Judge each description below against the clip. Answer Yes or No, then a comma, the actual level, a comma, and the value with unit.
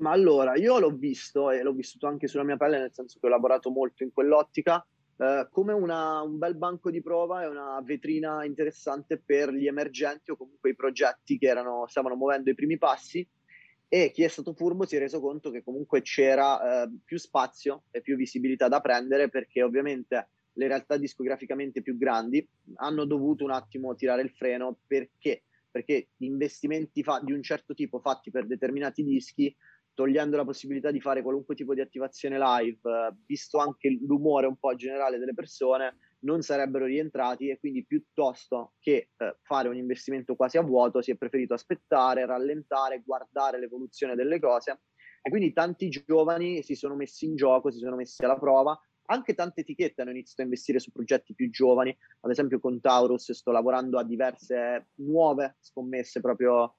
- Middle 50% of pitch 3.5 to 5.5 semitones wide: No, average, 2.8 semitones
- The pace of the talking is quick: Yes, fast, 180 wpm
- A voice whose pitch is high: No, medium, 140 Hz